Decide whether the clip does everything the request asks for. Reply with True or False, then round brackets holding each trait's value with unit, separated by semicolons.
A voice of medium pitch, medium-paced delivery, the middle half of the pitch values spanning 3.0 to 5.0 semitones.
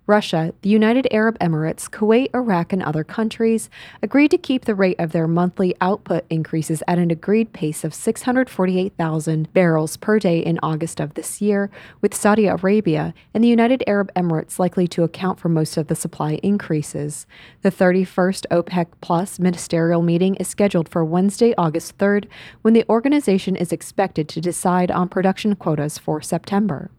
True (180 Hz; 165 wpm; 3.9 semitones)